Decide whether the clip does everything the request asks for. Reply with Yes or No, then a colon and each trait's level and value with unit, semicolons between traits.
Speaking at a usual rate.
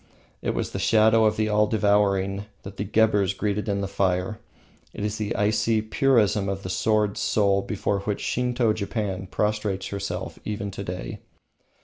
Yes: average, 165 wpm